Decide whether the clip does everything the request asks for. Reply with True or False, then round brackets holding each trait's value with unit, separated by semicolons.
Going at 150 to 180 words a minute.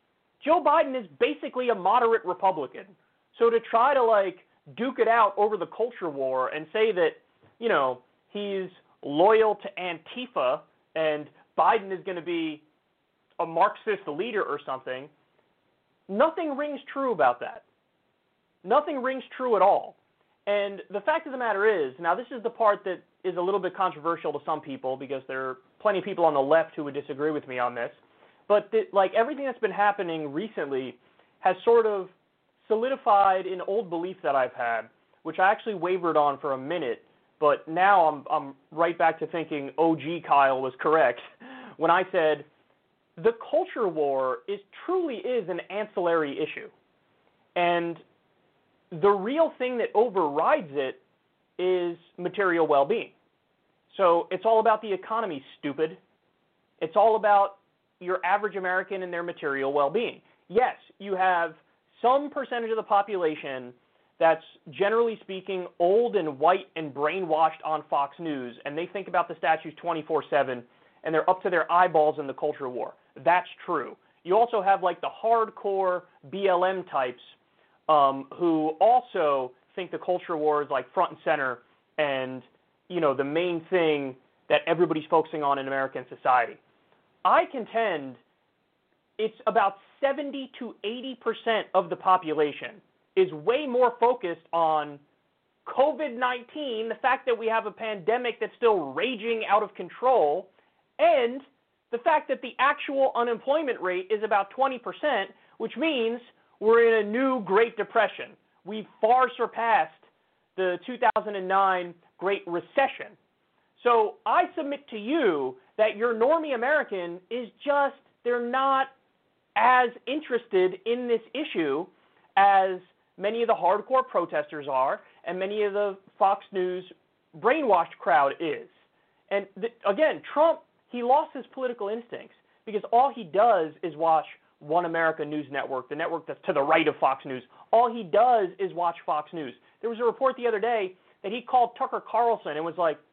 True (160 wpm)